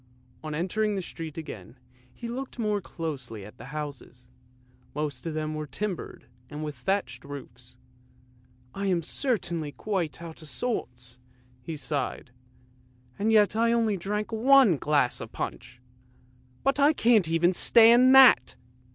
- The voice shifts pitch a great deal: Yes, wide, 8.4 semitones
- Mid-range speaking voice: Yes, medium, 160 Hz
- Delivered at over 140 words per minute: Yes, average, 150 wpm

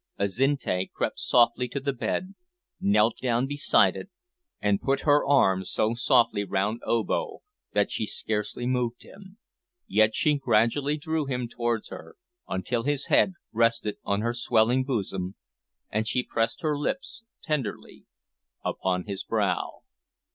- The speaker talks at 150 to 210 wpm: No, average, 140 wpm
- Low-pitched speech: Yes, low, 120 Hz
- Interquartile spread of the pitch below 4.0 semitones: No, average, 4.6 semitones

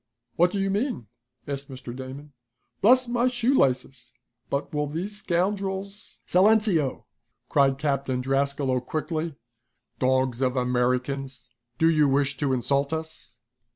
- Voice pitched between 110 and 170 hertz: Yes, medium, 140 Hz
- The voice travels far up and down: Yes, wide, 6.0 semitones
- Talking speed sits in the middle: No, slow, 125 wpm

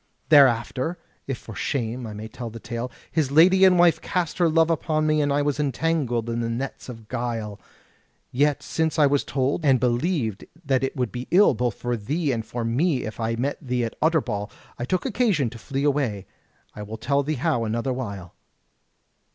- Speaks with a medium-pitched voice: No, low, 130 Hz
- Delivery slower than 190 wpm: No, average, 200 wpm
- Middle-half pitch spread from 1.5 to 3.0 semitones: No, average, 4.7 semitones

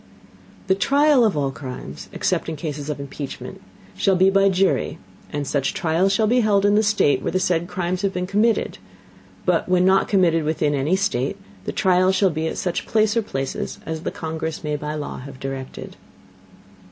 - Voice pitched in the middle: Yes, medium, 180 Hz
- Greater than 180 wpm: Yes, average, 195 wpm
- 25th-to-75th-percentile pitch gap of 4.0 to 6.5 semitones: Yes, average, 4.7 semitones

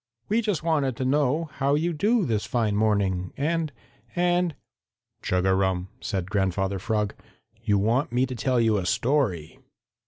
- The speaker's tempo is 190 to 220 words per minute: No, average, 165 wpm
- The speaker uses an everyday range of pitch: No, wide, 7.2 semitones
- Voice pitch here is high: No, low, 120 Hz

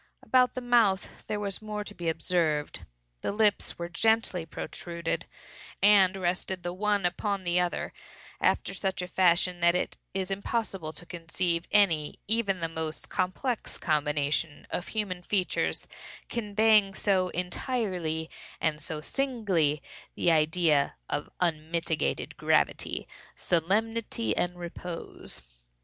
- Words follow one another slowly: Yes, slow, 125 wpm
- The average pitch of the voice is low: No, medium, 180 Hz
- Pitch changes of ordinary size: Yes, average, 3.8 semitones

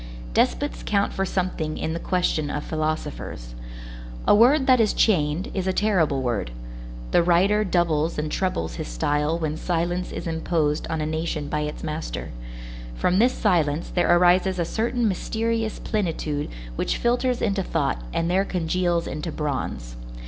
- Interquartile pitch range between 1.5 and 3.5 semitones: No, average, 4.1 semitones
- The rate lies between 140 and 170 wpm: Yes, average, 155 wpm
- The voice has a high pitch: No, medium, 170 Hz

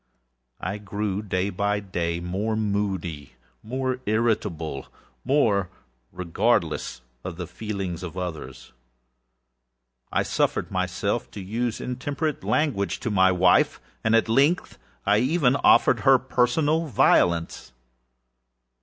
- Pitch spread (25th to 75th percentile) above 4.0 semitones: Yes, average, 5.1 semitones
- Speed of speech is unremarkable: No, slow, 110 wpm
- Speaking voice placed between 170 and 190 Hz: No, low, 105 Hz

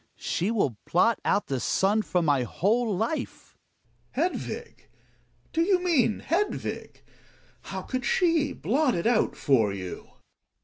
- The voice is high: Yes, high, 225 Hz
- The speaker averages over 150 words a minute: No, slow, 135 wpm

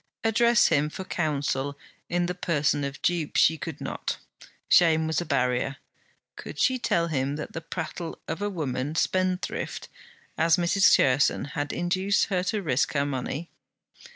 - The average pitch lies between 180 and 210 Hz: No, medium, 160 Hz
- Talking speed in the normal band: Yes, average, 155 wpm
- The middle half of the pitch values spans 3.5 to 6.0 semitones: Yes, average, 4.1 semitones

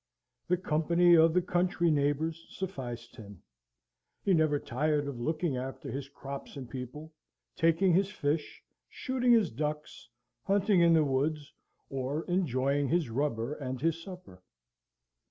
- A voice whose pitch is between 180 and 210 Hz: No, medium, 150 Hz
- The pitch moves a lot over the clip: No, average, 4.2 semitones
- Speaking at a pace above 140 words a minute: No, slow, 135 wpm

